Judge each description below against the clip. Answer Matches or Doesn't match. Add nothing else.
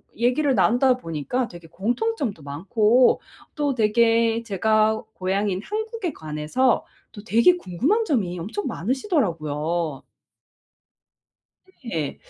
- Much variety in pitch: Matches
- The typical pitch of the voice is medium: Doesn't match